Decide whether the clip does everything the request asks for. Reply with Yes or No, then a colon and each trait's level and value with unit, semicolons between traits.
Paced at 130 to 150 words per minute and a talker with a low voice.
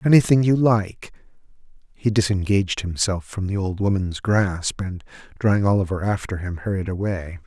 Yes: average, 145 wpm; low, 100 Hz